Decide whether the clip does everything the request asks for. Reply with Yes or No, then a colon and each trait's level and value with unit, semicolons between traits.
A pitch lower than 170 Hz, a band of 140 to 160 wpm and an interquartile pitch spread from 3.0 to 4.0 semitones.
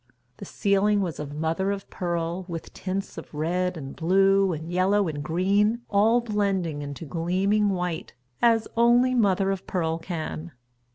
No: medium, 185 Hz; average, 155 wpm; average, 3.5 semitones